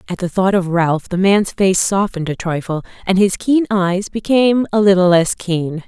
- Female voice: Yes, female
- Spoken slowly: No, fast, 205 wpm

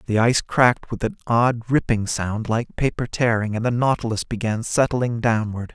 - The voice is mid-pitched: No, low, 115 Hz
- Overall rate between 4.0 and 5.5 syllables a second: Yes, 5.0 syllables/s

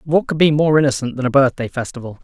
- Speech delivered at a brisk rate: Yes, fast, 240 wpm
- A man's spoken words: Yes, male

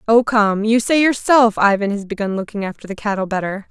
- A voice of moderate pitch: No, high, 215 Hz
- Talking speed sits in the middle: No, fast, 210 wpm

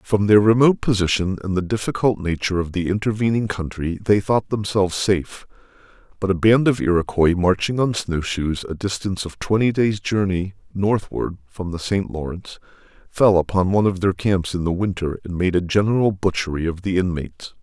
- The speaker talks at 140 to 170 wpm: No, average, 180 wpm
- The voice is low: Yes, very low, 95 Hz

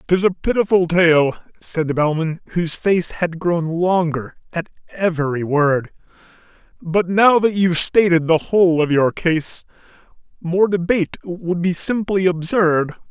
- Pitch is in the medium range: Yes, medium, 170 Hz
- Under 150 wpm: Yes, average, 140 wpm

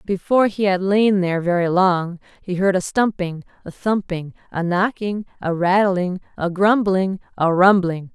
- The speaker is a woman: Yes, female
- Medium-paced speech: Yes, average, 155 wpm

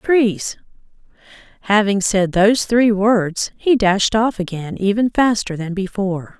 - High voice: Yes, high, 205 Hz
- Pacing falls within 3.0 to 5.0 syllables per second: Yes, 4.0 syllables/s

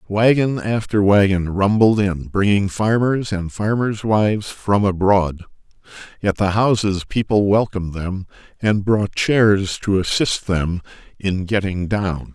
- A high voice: No, low, 100 Hz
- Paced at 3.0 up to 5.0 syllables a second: Yes, 4.0 syllables/s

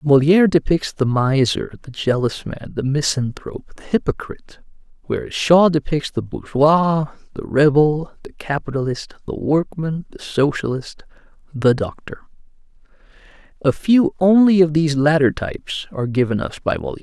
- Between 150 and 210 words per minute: No, slow, 135 wpm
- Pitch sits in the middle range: Yes, medium, 150 Hz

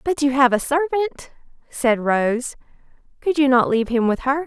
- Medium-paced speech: Yes, average, 190 wpm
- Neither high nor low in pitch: No, very high, 270 Hz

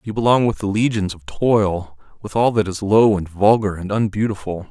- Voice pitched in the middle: No, low, 100 Hz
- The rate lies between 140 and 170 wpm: No, fast, 205 wpm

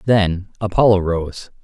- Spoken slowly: Yes, slow, 110 wpm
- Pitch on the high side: No, very low, 95 Hz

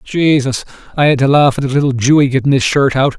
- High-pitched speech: No, low, 135 Hz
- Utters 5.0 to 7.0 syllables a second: Yes, 6.1 syllables/s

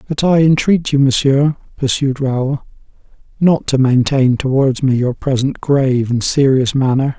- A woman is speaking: No, male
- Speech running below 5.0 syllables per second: Yes, 4.5 syllables/s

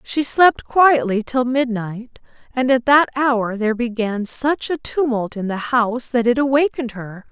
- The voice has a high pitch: Yes, high, 245 Hz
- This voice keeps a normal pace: Yes, average, 170 wpm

